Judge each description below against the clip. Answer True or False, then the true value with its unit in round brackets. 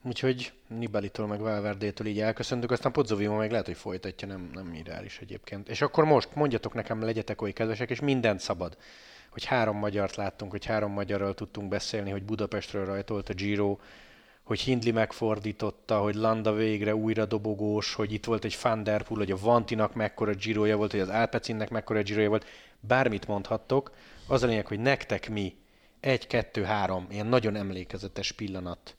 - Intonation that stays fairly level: True (1.8 semitones)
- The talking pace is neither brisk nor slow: False (170 wpm)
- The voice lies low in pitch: True (105 Hz)